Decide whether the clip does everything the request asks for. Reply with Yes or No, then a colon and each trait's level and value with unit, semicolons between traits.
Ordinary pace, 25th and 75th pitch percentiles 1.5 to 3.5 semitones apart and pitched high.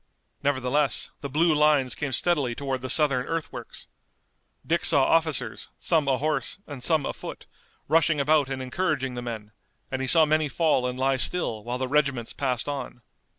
No: average, 165 wpm; average, 3.1 semitones; medium, 140 Hz